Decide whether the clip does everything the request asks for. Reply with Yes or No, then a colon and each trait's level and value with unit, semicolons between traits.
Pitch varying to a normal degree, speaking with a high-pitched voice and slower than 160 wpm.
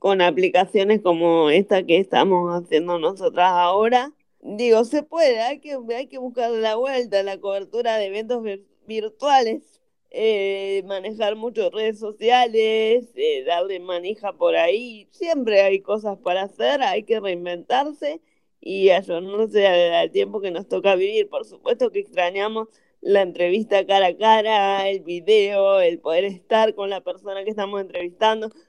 Yes: average, 3.7 semitones; high, 205 Hz; average, 150 wpm